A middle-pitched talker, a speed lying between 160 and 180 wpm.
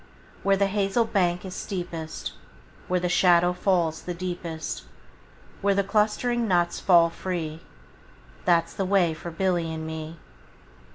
No: medium, 180 Hz; average, 150 wpm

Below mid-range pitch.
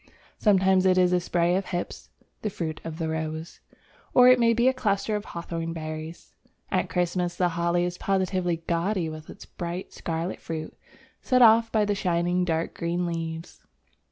No: medium, 175 Hz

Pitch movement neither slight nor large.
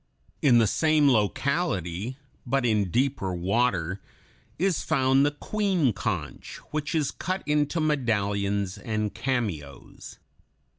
No: wide, 6.7 semitones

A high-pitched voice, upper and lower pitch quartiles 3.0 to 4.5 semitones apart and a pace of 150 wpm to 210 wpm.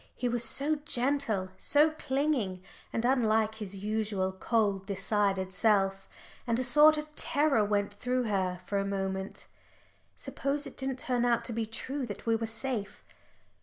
No: high, 225 Hz; average, 4.9 semitones; average, 160 wpm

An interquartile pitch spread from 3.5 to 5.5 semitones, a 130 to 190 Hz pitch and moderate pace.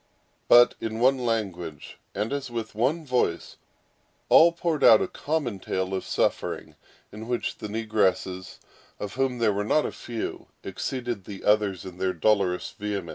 No: average, 4.3 semitones; low, 110 Hz; average, 160 wpm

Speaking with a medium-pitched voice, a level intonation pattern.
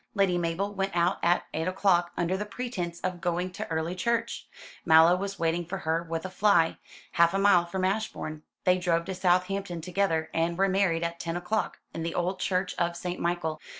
Yes: medium, 175 Hz; narrow, 2.3 semitones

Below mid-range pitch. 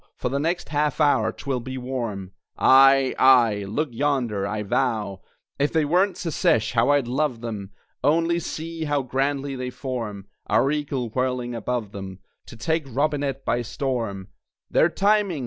Yes: low, 130 Hz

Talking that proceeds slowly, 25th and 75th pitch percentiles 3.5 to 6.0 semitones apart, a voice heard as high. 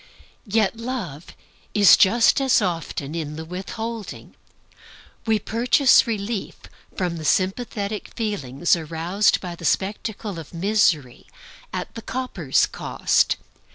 Yes: slow, 115 wpm; average, 5.0 semitones; high, 195 Hz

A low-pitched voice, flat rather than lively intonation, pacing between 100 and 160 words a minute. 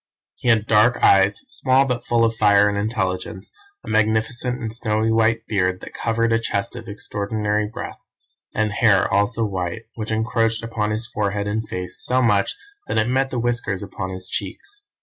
No: low, 110 Hz; narrow, 2.2 semitones; average, 180 wpm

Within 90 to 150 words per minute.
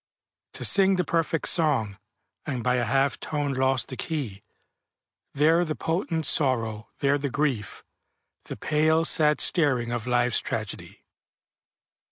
Yes: slow, 135 wpm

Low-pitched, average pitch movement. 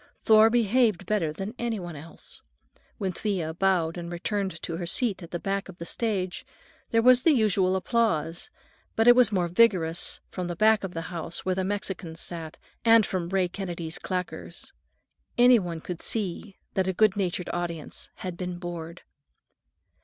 No: medium, 185 Hz; average, 3.7 semitones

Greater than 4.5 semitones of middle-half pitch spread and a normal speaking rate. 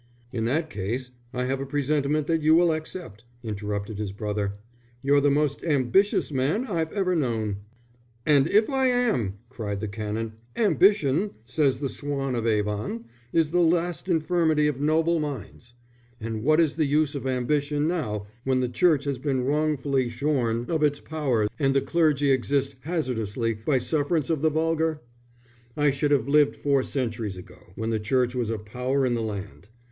Yes: average, 5.0 semitones; average, 170 wpm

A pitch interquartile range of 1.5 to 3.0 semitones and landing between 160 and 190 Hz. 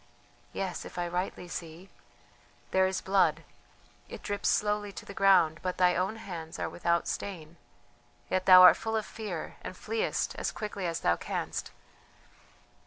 Yes: average, 2.7 semitones; medium, 185 Hz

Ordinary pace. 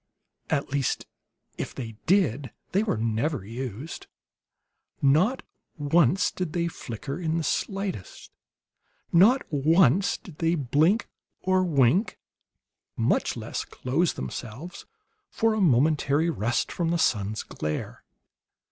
No: slow, 115 wpm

